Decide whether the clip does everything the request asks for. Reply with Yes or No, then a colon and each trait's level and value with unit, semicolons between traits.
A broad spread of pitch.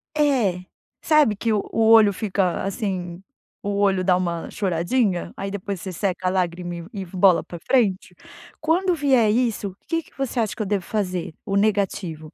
No: average, 3.7 semitones